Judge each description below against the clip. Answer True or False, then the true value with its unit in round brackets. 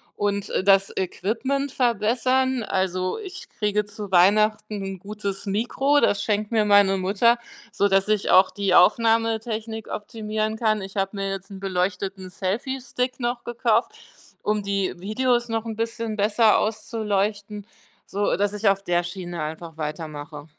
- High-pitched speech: True (210 Hz)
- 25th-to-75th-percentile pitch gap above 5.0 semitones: False (2.7 semitones)